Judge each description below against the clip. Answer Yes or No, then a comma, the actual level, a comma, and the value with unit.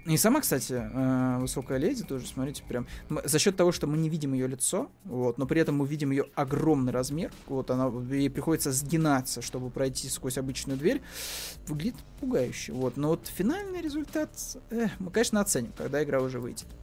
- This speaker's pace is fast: Yes, fast, 180 wpm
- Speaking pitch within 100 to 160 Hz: Yes, medium, 140 Hz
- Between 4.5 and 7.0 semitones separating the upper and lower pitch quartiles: No, average, 3.8 semitones